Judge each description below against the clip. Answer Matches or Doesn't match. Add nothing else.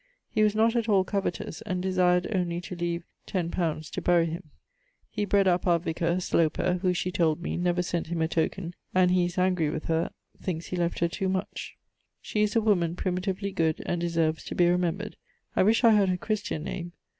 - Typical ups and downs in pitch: Doesn't match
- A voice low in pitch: Doesn't match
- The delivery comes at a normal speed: Doesn't match